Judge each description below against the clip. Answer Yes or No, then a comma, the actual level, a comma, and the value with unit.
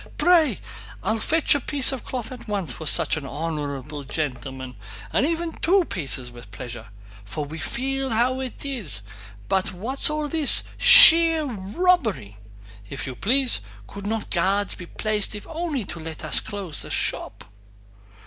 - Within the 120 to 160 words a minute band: Yes, average, 155 wpm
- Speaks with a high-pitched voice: Yes, high, 210 Hz